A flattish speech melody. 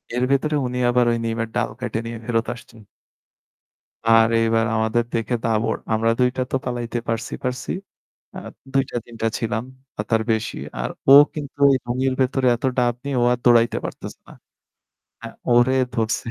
Yes: narrow, 1.8 semitones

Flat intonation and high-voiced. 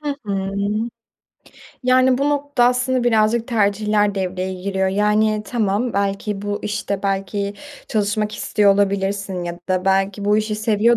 Yes: narrow, 2.2 semitones; high, 205 Hz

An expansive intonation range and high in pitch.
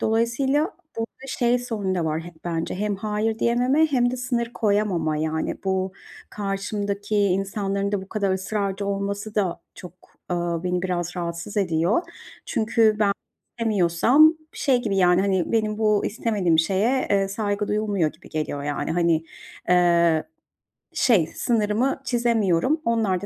No: average, 4.1 semitones; high, 200 Hz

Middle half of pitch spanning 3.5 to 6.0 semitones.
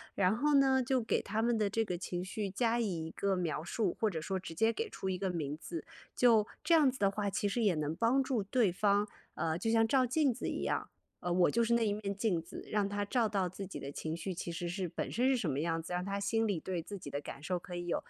Yes: average, 4.5 semitones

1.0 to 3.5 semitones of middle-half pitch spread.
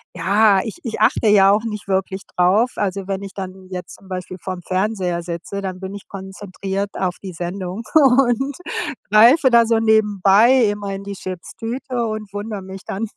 Yes: average, 2.7 semitones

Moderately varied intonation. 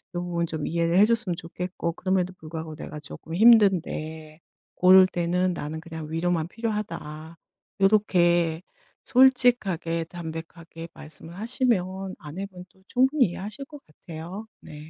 Yes: average, 3.4 semitones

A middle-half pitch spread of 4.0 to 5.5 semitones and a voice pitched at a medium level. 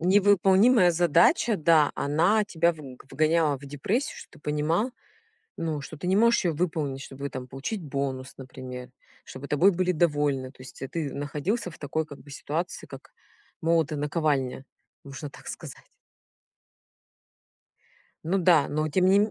Yes: average, 4.3 semitones; medium, 155 Hz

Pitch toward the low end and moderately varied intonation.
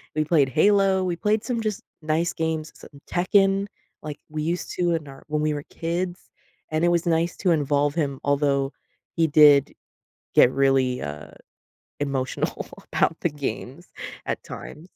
No: medium, 155 Hz; average, 3.5 semitones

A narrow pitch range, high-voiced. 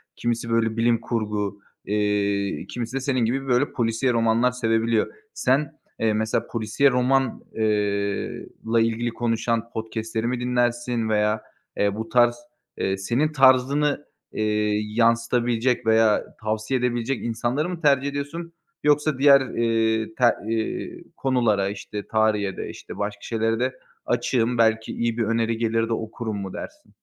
No: narrow, 2.2 semitones; low, 115 Hz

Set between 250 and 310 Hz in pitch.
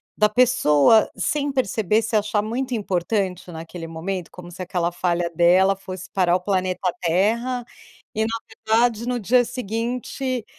No: high, 205 Hz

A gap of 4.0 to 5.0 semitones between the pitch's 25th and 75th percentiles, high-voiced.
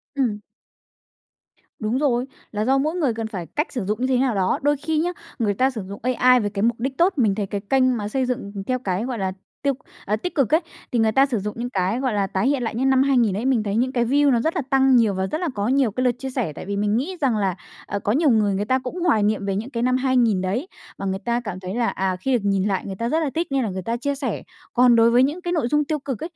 Yes: average, 4.5 semitones; high, 240 Hz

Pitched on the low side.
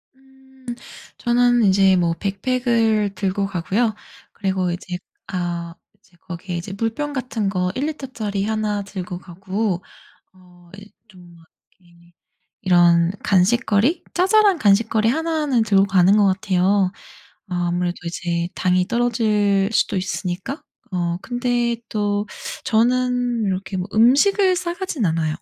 No: high, 200 Hz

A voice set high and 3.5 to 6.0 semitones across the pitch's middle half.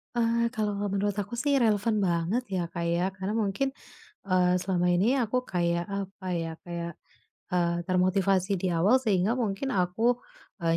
Yes: high, 195 Hz; average, 4.2 semitones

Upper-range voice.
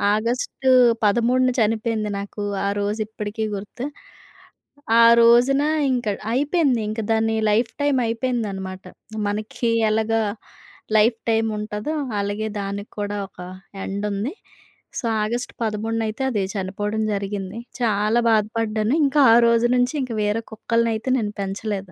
Yes: high, 220 Hz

